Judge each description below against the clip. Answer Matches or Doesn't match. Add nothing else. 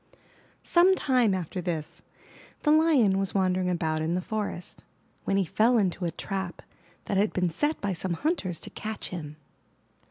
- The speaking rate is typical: Matches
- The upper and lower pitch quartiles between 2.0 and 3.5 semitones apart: Doesn't match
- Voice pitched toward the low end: Doesn't match